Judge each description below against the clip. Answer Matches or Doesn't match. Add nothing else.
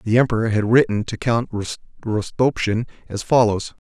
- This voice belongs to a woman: Doesn't match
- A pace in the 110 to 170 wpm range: Matches